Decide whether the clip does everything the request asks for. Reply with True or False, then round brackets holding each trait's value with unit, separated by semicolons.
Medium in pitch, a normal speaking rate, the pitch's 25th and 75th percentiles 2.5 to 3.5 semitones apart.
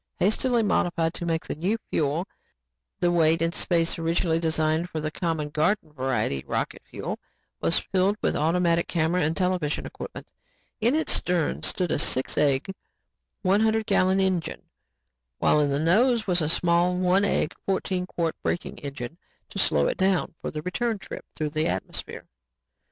True (170 Hz; 170 wpm; 3.2 semitones)